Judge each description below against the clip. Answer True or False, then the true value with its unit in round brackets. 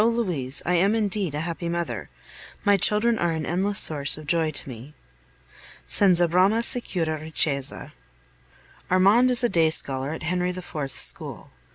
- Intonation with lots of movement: False (4.5 semitones)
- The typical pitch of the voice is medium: True (175 Hz)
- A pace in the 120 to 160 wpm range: True (155 wpm)